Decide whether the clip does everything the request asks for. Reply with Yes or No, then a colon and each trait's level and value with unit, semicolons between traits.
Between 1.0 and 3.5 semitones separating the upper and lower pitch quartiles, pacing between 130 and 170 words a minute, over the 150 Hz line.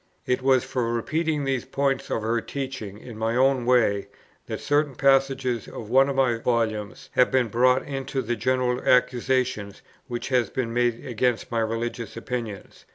No: narrow, 2.5 semitones; average, 165 wpm; low, 125 Hz